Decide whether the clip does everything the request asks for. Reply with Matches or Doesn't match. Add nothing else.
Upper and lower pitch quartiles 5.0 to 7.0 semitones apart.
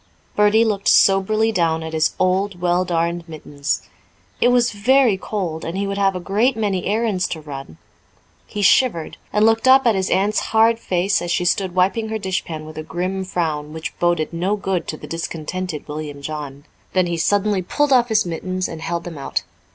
Doesn't match